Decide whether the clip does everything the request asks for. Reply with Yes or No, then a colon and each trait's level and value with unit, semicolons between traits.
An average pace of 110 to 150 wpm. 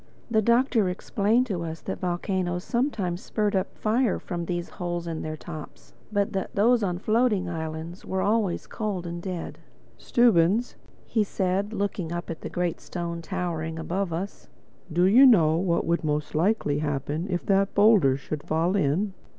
No: average, 165 wpm